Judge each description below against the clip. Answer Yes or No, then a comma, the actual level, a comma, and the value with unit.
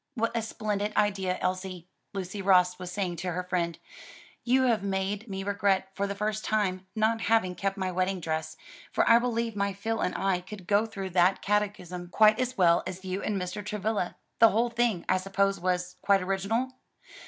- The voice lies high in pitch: Yes, high, 195 Hz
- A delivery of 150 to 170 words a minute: No, average, 190 wpm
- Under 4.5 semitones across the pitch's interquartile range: Yes, average, 2.7 semitones